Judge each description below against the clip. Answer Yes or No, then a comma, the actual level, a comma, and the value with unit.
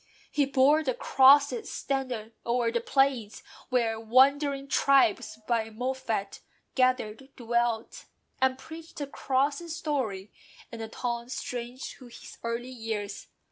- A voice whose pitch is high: Yes, very high, 255 Hz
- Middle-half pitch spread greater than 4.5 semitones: No, average, 3.1 semitones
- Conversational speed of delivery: No, slow, 125 wpm